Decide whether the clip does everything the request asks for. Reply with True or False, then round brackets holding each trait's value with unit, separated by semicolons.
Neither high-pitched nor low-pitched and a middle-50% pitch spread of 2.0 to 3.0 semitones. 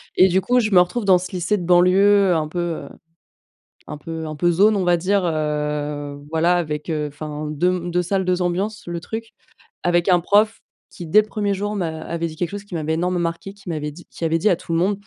False (175 Hz; 3.4 semitones)